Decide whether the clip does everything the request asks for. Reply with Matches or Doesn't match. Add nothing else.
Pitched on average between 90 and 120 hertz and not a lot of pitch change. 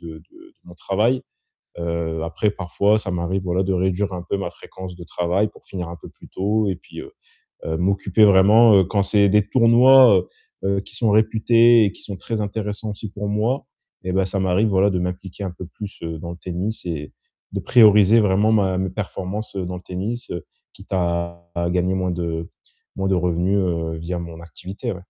Doesn't match